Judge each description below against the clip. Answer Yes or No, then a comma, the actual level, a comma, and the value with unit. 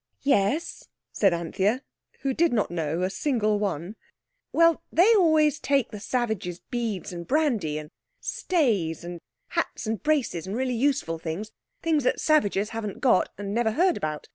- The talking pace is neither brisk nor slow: Yes, average, 155 wpm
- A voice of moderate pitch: No, high, 220 Hz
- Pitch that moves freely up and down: Yes, wide, 7.9 semitones